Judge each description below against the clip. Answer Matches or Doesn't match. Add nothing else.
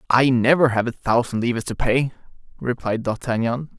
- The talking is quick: Doesn't match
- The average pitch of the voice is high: Doesn't match